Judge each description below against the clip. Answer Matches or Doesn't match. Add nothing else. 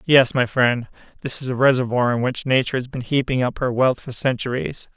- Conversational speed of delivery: Doesn't match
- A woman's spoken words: Doesn't match